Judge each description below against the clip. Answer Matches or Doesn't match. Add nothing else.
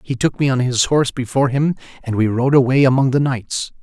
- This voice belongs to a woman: Doesn't match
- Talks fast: Matches